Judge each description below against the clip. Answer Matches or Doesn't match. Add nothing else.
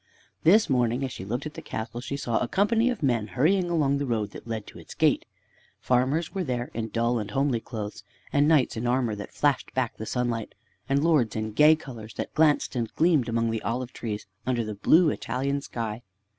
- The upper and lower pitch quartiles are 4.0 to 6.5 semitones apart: Matches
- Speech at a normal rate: Doesn't match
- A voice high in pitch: Doesn't match